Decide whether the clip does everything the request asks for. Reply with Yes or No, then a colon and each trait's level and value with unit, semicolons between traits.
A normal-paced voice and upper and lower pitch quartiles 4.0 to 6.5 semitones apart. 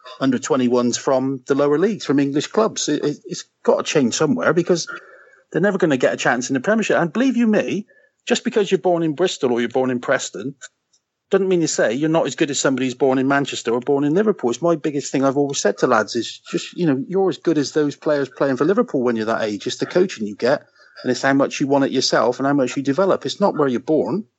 No: fast, 270 wpm; wide, 5.5 semitones